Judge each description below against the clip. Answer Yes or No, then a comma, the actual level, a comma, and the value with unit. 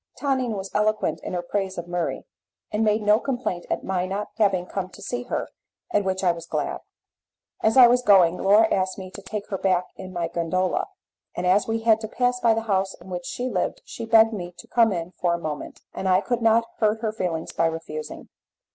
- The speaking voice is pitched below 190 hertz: No, high, 195 Hz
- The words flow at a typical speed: No, fast, 225 wpm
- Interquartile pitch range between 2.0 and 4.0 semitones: Yes, average, 3.7 semitones